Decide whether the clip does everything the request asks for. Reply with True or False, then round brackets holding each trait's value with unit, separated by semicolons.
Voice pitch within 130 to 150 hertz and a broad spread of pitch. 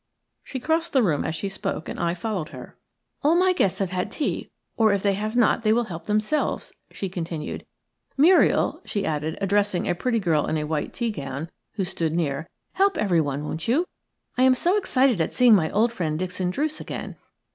False (200 Hz; 6.6 semitones)